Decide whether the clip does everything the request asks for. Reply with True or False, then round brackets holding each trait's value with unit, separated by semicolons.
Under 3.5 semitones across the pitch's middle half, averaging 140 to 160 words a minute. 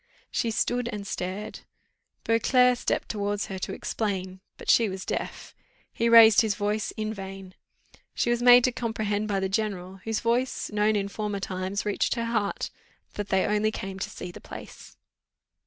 False (2.8 semitones; 170 wpm)